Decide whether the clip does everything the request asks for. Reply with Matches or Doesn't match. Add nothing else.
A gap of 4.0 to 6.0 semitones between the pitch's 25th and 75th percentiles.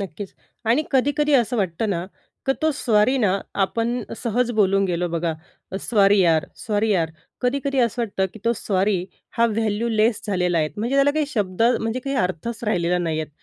Matches